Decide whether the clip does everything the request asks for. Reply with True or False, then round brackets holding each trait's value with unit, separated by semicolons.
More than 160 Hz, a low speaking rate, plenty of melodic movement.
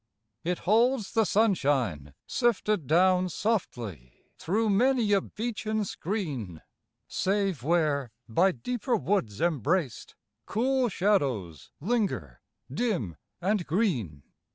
True (185 Hz; 100 wpm; 8.7 semitones)